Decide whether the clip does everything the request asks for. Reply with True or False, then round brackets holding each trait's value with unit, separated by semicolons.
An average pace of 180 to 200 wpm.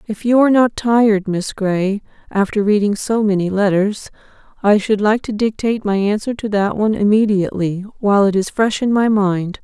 True (185 wpm)